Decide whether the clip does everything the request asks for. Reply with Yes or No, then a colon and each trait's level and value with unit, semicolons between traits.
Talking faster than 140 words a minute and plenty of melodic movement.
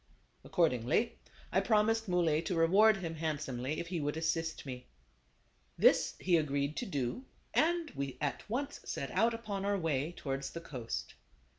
Yes: average, 155 wpm; wide, 6.5 semitones